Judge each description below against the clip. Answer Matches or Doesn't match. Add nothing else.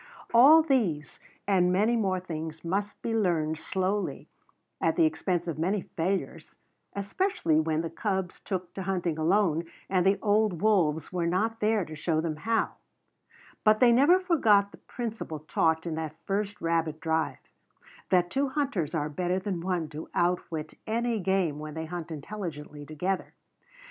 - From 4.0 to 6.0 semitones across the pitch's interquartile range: Matches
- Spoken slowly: Doesn't match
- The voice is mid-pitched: Matches